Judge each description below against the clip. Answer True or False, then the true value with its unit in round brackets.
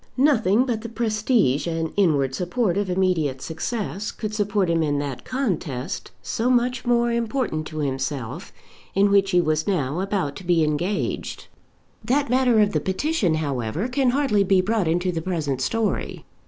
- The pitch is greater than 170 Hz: True (190 Hz)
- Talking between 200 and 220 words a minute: False (165 wpm)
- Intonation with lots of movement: True (6.5 semitones)